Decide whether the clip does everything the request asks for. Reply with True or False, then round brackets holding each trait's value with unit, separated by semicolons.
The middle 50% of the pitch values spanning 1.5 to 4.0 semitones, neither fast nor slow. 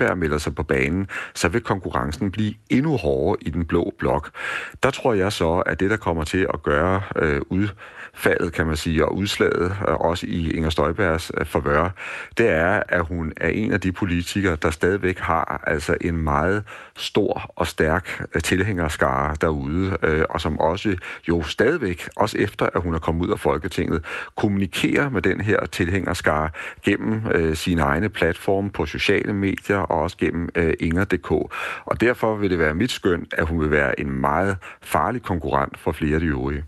True (3.5 semitones; 180 wpm)